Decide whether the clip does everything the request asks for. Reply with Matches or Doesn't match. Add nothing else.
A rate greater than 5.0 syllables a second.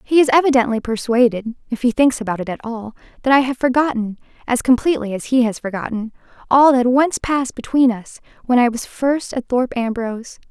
Matches